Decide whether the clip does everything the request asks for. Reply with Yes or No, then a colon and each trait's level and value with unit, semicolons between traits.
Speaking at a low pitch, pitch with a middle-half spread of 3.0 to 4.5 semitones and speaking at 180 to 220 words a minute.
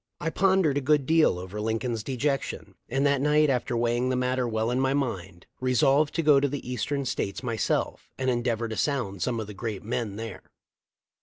Yes: low, 125 Hz; average, 3.9 semitones; average, 190 wpm